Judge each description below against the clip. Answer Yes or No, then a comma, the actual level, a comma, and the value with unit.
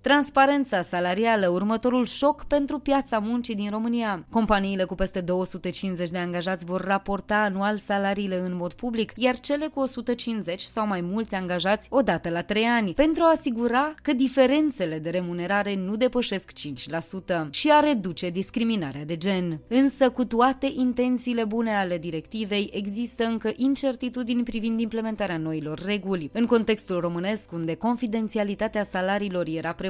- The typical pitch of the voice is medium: No, high, 210 Hz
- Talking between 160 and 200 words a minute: No, average, 145 wpm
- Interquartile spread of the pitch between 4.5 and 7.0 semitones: Yes, average, 4.9 semitones